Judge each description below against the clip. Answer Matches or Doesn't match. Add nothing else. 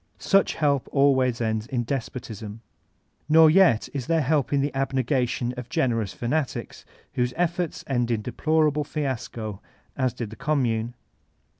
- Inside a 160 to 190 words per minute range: Doesn't match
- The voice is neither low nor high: Doesn't match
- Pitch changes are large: Doesn't match